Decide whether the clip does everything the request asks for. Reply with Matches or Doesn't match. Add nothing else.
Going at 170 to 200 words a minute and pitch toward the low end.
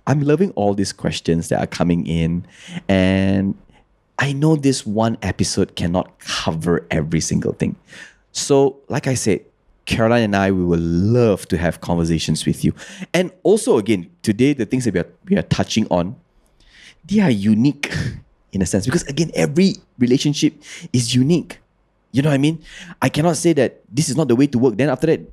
Matches